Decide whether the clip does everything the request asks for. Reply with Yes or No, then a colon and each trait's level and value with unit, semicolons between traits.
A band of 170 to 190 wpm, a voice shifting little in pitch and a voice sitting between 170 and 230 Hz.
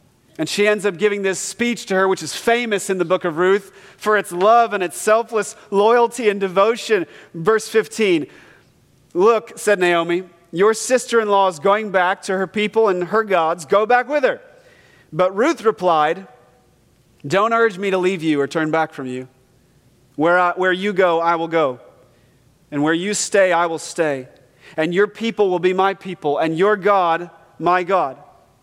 No: average, 185 wpm; average, 4.3 semitones; high, 190 Hz